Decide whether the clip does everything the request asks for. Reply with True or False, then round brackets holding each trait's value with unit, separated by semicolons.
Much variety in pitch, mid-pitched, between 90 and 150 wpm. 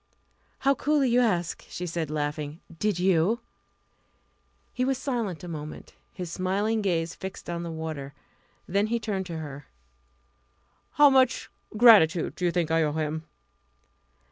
True (5.8 semitones; 175 Hz; 145 wpm)